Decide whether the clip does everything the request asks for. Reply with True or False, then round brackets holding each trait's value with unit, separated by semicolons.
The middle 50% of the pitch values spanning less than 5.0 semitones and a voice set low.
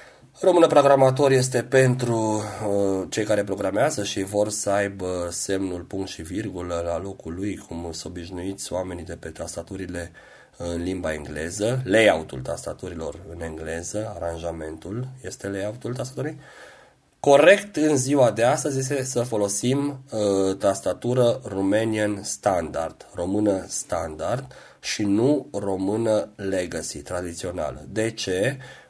False (5.6 semitones; 100 Hz)